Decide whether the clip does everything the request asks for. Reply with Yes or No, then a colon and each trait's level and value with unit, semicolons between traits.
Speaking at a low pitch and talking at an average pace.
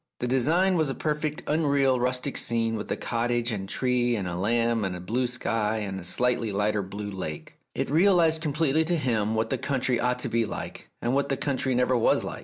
No: low, 125 Hz; fast, 220 wpm